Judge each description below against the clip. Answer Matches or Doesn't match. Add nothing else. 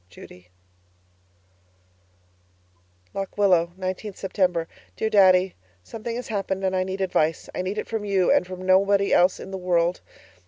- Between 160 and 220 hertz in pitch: Matches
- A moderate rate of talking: Matches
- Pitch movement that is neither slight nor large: Doesn't match